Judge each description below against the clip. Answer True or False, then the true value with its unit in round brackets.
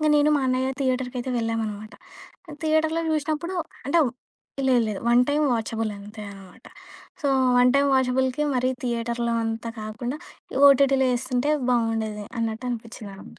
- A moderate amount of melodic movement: True (3.2 semitones)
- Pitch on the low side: False (245 Hz)